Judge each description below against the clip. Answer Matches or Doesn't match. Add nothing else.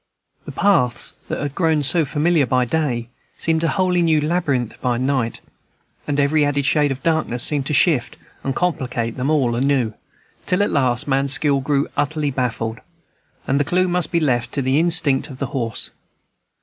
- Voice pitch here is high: Doesn't match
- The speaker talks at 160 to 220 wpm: Matches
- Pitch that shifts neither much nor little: Matches